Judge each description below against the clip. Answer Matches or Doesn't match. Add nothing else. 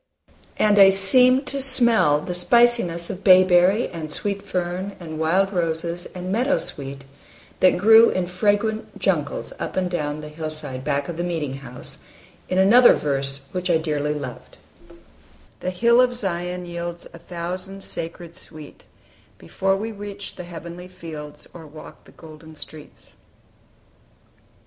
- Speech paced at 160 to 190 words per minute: Doesn't match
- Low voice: Doesn't match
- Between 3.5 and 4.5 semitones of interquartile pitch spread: Matches